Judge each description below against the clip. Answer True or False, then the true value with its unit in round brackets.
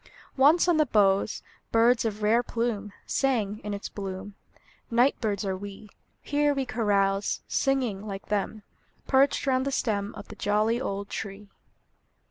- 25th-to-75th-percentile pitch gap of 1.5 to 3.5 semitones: False (4.0 semitones)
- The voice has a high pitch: True (215 Hz)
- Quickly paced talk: False (150 wpm)